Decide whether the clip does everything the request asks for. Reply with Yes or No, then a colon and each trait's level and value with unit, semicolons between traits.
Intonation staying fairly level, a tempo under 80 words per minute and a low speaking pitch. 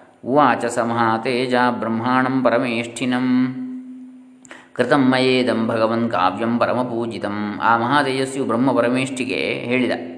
Yes: narrow, 2.3 semitones; average, 70 wpm; low, 125 Hz